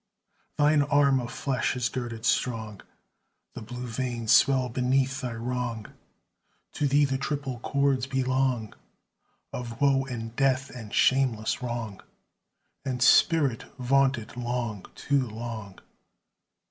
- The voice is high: No, low, 125 Hz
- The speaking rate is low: Yes, slow, 120 wpm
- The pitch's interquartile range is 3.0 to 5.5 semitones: No, narrow, 2.5 semitones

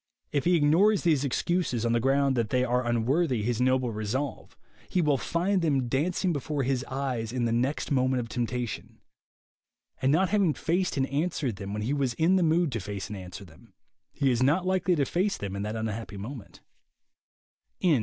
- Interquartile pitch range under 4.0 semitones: No, wide, 5.6 semitones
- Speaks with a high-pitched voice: No, low, 130 Hz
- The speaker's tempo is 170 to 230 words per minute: Yes, average, 195 wpm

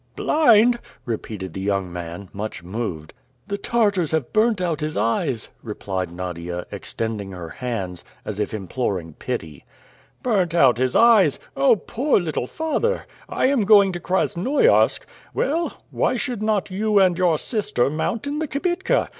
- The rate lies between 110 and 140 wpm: No, average, 150 wpm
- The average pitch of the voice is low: No, medium, 160 Hz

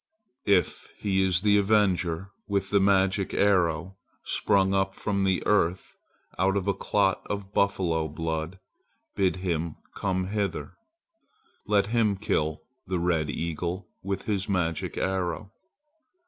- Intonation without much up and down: Yes, narrow, 2.3 semitones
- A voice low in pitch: Yes, very low, 95 Hz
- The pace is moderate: No, slow, 130 wpm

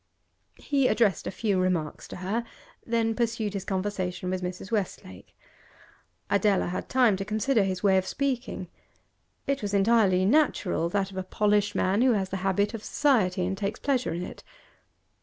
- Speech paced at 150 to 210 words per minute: Yes, average, 170 wpm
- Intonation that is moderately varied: Yes, average, 3.5 semitones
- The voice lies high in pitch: Yes, high, 200 Hz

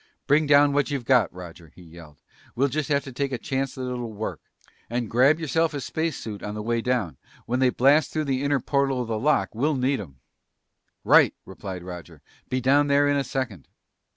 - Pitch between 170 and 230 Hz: No, low, 130 Hz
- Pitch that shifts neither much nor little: Yes, average, 4.5 semitones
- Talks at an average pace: No, fast, 210 wpm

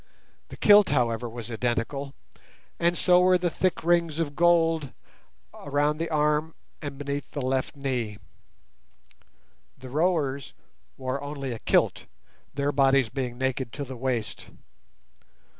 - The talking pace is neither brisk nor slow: No, slow, 130 wpm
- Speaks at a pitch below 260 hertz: Yes, medium, 140 Hz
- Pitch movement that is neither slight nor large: Yes, average, 3.8 semitones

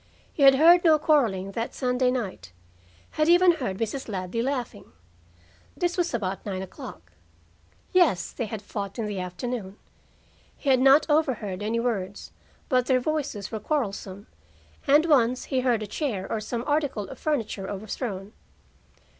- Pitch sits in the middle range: No, high, 235 Hz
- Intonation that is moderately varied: No, wide, 6.0 semitones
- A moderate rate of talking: Yes, average, 155 wpm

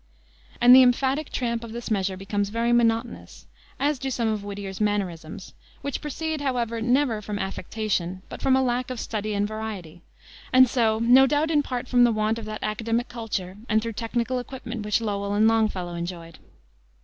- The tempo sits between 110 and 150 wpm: No, average, 185 wpm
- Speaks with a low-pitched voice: No, high, 225 Hz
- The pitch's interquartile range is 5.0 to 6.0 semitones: No, average, 3.3 semitones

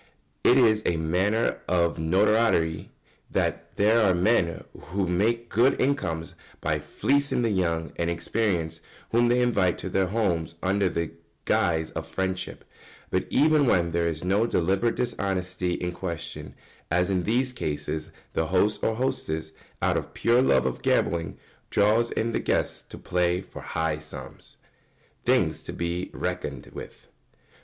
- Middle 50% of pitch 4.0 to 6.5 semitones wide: Yes, average, 5.1 semitones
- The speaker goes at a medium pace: Yes, average, 150 wpm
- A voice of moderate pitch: No, very low, 90 Hz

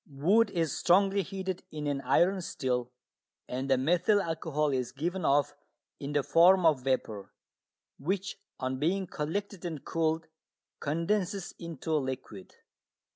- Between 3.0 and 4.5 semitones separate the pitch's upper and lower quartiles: No, average, 5.2 semitones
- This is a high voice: No, medium, 160 Hz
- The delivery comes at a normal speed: No, slow, 130 wpm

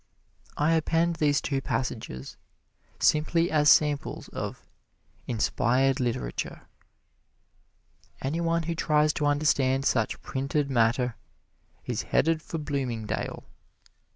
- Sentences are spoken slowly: Yes, slow, 100 wpm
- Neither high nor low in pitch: Yes, medium, 145 Hz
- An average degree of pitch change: Yes, average, 3.4 semitones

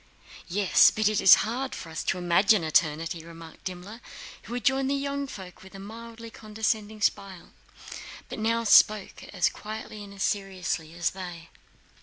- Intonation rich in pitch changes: No, average, 4.0 semitones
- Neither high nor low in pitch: No, high, 200 Hz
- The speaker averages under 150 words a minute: No, average, 160 wpm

